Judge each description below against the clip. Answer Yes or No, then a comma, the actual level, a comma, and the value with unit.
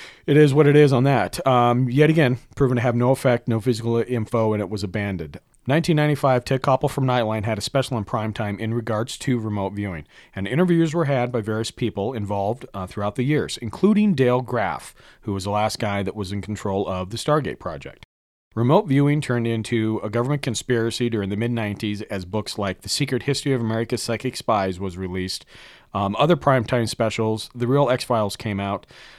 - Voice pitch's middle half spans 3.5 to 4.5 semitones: Yes, average, 4.0 semitones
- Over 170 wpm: Yes, average, 200 wpm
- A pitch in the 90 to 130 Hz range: Yes, low, 115 Hz